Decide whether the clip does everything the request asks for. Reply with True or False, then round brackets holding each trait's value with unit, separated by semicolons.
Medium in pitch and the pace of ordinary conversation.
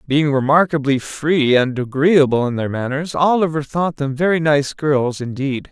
True (145 Hz; 155 wpm)